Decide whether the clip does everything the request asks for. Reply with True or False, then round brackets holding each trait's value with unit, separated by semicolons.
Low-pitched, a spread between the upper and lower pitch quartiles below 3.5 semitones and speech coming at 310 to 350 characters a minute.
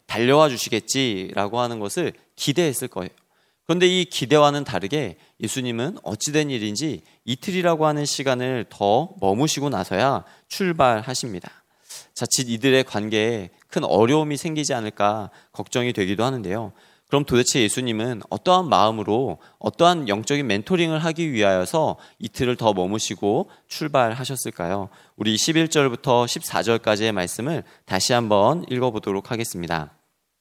False (120 Hz; 5.5 semitones; 330 characters per minute)